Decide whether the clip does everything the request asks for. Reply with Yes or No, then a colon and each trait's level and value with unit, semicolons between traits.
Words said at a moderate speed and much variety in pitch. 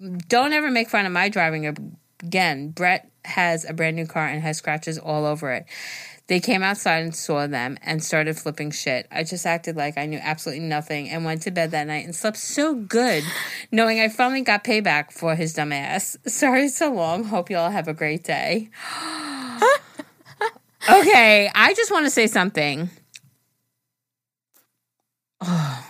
Yes: average, 175 wpm; wide, 6.5 semitones